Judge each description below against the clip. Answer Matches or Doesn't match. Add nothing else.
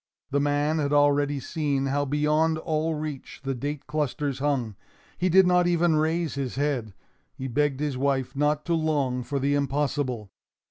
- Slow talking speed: Doesn't match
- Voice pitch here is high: Doesn't match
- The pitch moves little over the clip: Matches